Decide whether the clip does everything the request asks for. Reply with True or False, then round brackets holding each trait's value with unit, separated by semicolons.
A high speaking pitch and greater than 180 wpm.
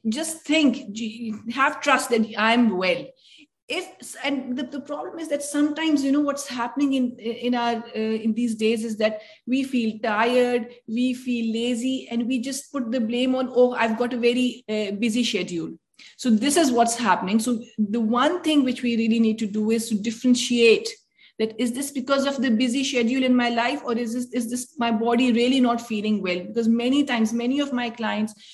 True (245 Hz; 200 wpm)